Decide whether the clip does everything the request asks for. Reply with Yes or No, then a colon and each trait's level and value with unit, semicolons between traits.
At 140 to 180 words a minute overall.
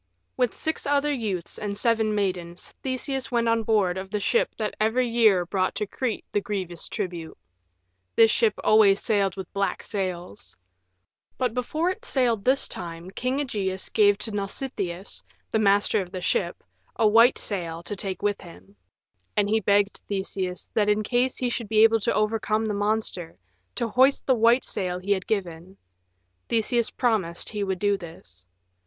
Yes: average, 170 wpm